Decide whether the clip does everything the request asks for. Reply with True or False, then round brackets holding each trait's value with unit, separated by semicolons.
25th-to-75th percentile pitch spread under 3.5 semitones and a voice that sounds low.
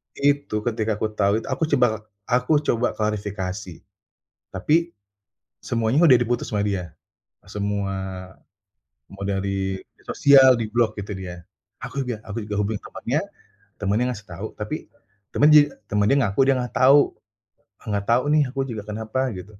False (3.8 semitones; 110 Hz)